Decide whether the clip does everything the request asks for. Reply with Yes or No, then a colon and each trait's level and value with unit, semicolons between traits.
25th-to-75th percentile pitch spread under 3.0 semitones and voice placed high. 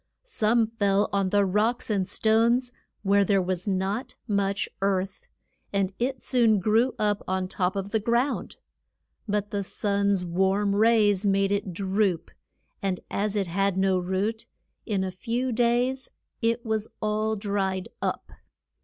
Yes: narrow, 2.4 semitones; high, 200 Hz